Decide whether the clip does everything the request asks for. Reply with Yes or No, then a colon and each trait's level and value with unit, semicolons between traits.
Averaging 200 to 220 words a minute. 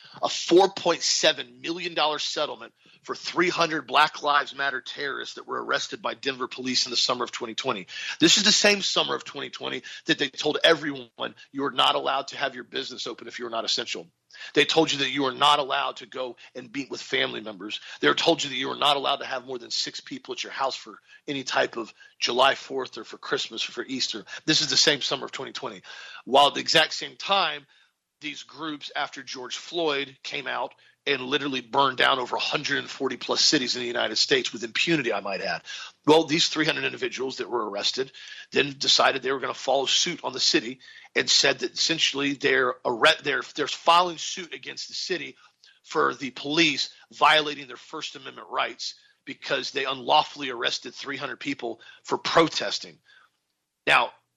No: average, 190 wpm